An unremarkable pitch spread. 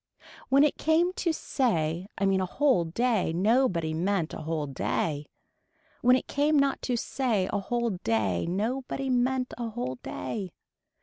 No: wide, 7.7 semitones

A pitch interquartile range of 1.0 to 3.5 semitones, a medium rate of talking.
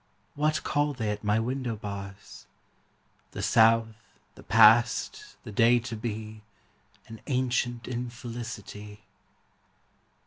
No: narrow, 2.4 semitones; slow, 105 wpm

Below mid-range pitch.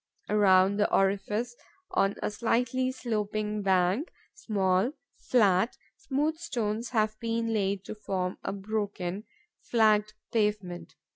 No: high, 210 Hz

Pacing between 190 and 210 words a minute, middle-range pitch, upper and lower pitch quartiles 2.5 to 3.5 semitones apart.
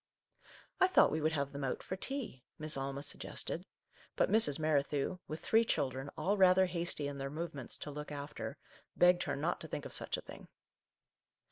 No: average, 200 wpm; medium, 155 Hz; average, 4.1 semitones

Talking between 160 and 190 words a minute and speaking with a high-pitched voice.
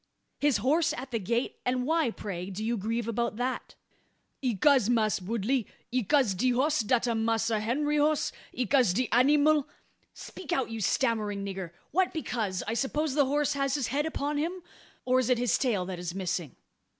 Yes: average, 185 wpm; high, 245 Hz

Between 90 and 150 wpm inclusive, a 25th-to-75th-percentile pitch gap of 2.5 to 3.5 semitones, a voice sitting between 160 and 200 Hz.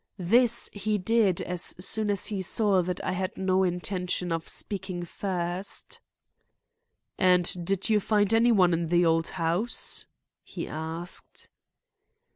Yes: slow, 135 wpm; average, 2.8 semitones; medium, 185 Hz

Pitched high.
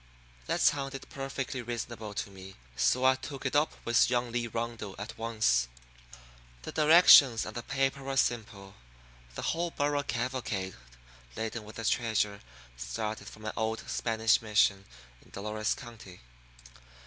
No: low, 115 Hz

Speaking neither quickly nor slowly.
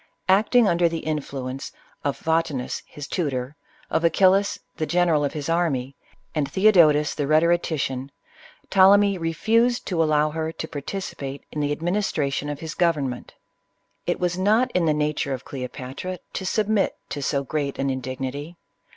Yes: average, 150 wpm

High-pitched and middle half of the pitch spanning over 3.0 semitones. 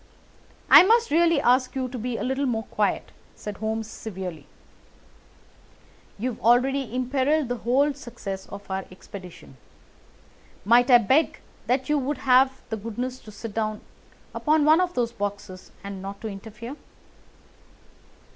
Yes: high, 240 Hz; average, 4.3 semitones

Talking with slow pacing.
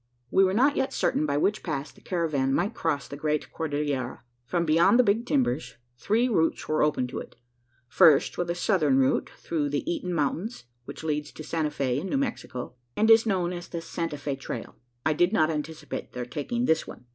No: fast, 205 wpm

